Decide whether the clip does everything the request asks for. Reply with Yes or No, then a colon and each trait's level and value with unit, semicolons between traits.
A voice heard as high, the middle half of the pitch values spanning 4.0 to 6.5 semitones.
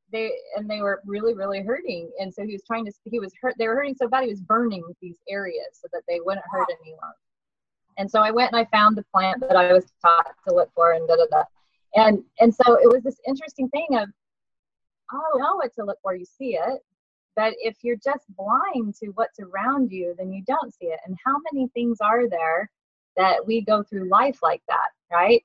Yes: high, 215 Hz; average, 4.6 semitones